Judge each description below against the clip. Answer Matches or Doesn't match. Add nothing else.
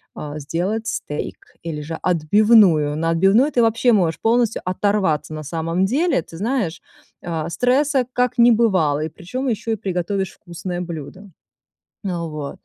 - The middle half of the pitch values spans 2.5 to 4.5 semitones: Doesn't match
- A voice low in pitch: Doesn't match